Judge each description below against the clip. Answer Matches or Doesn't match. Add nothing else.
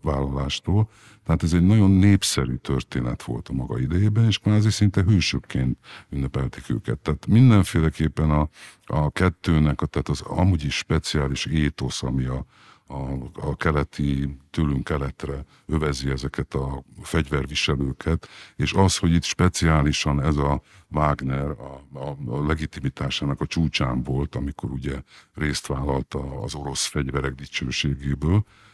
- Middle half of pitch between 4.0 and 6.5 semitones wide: Matches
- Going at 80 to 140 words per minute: Matches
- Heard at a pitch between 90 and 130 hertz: Doesn't match